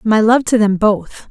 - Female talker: Yes, female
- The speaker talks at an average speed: No, fast, 230 wpm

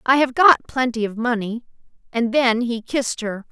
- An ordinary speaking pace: Yes, average, 190 wpm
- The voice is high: Yes, high, 240 Hz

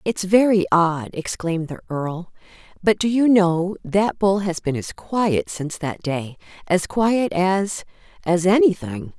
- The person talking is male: No, female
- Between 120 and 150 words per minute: Yes, average, 145 wpm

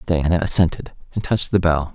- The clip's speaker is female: No, male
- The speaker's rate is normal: Yes, average, 185 wpm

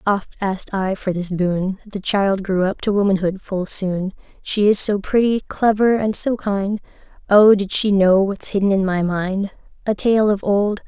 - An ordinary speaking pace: Yes, average, 195 wpm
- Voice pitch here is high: Yes, high, 200 Hz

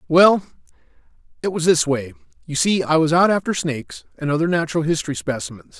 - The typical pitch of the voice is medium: Yes, medium, 160 Hz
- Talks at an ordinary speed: Yes, average, 175 wpm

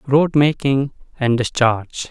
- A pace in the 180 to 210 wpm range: No, slow, 115 wpm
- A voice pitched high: No, low, 130 Hz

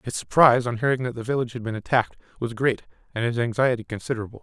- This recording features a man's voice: Yes, male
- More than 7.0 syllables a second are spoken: Yes, 7.7 syllables/s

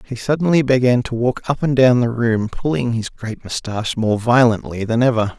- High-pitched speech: No, low, 120 Hz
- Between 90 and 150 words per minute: No, average, 200 wpm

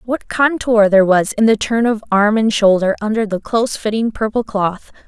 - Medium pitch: No, high, 215 Hz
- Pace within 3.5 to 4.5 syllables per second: No, 5.2 syllables/s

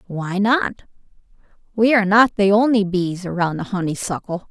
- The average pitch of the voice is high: Yes, high, 200 Hz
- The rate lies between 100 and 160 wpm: Yes, average, 145 wpm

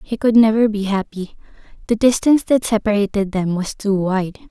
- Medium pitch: No, high, 210 Hz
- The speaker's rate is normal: Yes, average, 175 wpm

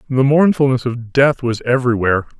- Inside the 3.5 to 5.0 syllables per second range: No, 5.7 syllables/s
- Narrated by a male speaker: Yes, male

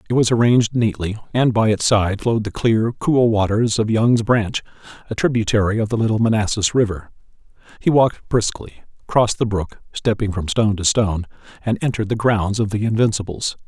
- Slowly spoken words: No, average, 180 wpm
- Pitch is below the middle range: Yes, low, 110 Hz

